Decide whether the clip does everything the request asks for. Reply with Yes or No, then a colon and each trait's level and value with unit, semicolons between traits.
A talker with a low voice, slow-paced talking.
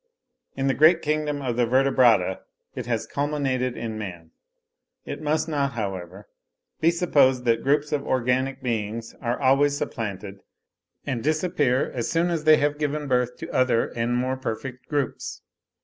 No: low, 130 Hz; average, 155 wpm